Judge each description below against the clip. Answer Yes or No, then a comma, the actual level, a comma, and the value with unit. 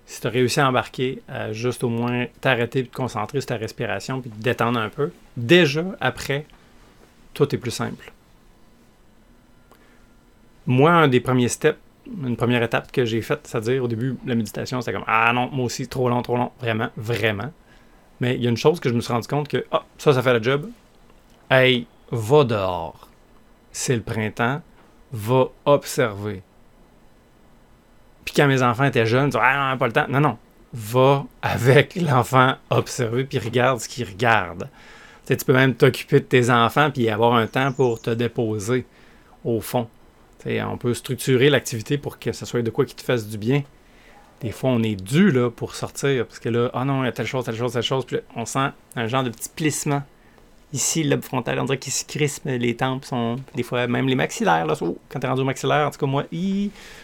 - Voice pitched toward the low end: Yes, low, 125 Hz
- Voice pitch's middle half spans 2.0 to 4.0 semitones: Yes, average, 2.7 semitones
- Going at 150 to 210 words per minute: No, fast, 220 wpm